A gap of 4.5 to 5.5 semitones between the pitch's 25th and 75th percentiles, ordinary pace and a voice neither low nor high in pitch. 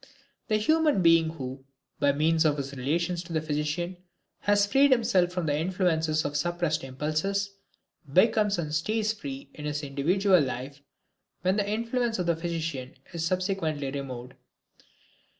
Yes: average, 4.9 semitones; average, 150 wpm; medium, 165 Hz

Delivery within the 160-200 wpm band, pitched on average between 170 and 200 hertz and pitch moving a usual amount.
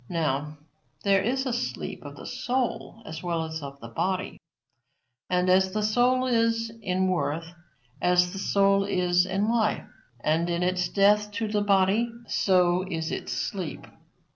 Yes: average, 165 wpm; high, 190 Hz; average, 3.3 semitones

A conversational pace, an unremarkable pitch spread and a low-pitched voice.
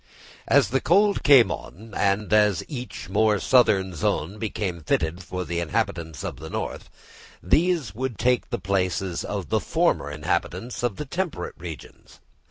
No: average, 155 wpm; wide, 6.1 semitones; low, 100 Hz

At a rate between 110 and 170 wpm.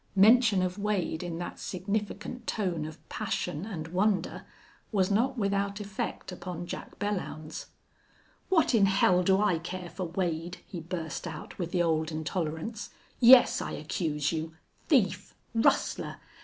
Yes: average, 140 wpm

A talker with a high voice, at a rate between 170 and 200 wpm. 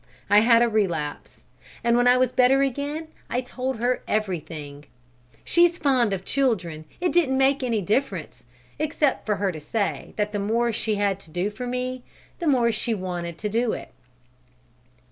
Yes: high, 235 Hz; average, 175 wpm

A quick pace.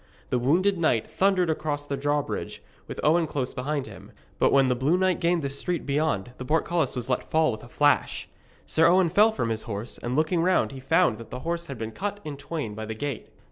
Yes: fast, 225 wpm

